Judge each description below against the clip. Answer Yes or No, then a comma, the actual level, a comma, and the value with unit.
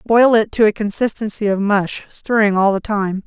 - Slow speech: No, average, 200 wpm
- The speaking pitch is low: No, high, 210 Hz